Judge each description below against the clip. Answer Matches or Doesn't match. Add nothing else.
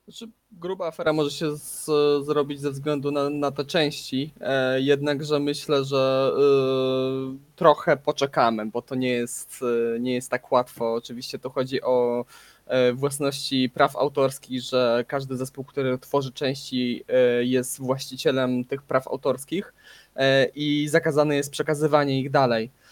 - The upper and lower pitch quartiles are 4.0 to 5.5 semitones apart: Doesn't match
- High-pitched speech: Doesn't match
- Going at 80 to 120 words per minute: Doesn't match